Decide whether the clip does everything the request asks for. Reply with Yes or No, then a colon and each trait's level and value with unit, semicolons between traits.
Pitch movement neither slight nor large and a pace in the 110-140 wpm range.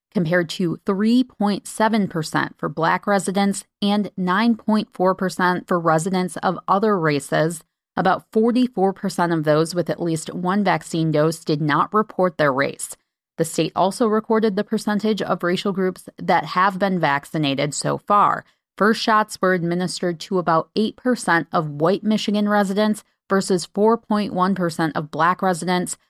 Yes: average, 3.7 semitones; slow, 135 wpm